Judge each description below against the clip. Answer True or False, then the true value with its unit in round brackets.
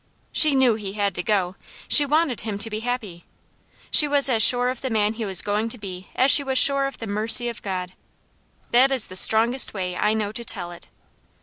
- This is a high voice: True (220 Hz)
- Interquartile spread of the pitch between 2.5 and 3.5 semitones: False (4.2 semitones)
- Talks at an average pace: False (225 wpm)